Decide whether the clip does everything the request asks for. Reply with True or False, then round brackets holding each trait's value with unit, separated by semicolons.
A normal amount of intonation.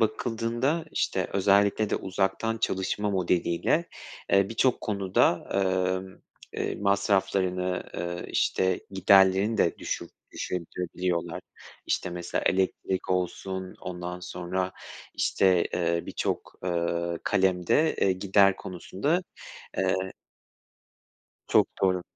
False (1.8 semitones)